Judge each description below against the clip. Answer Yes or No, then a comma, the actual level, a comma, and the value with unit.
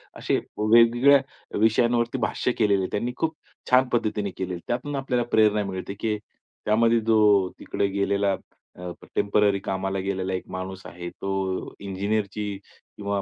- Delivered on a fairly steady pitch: No, average, 3.2 semitones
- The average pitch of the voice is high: No, low, 105 Hz